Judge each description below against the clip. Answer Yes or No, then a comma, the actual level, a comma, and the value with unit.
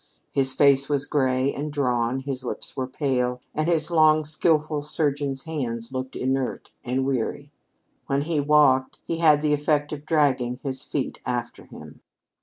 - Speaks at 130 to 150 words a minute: No, average, 160 wpm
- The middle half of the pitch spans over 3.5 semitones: No, narrow, 2.5 semitones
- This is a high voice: No, medium, 140 Hz